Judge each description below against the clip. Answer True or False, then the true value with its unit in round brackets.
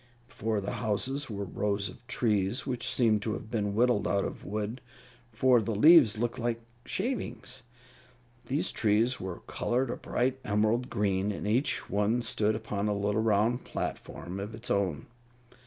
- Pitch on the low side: True (110 Hz)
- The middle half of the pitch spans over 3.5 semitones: False (3.0 semitones)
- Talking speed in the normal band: True (160 wpm)